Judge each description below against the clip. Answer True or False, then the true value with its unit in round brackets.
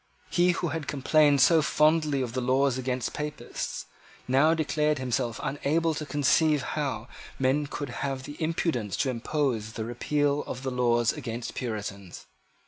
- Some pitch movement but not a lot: True (3.5 semitones)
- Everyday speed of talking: True (150 wpm)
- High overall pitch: False (135 Hz)